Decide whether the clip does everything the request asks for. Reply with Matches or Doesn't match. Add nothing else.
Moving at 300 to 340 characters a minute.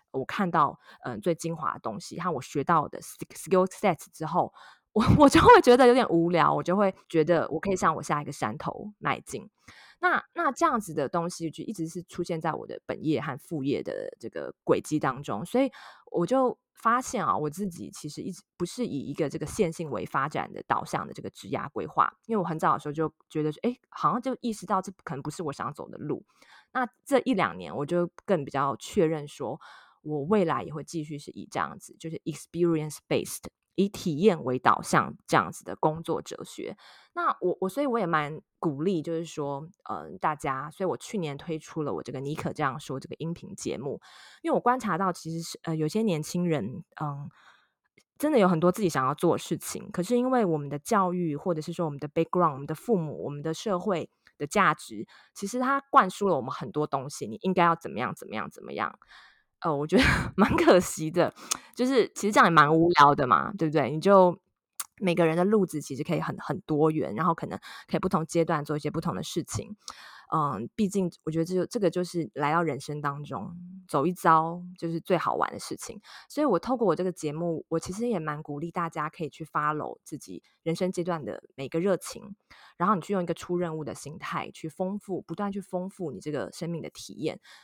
Matches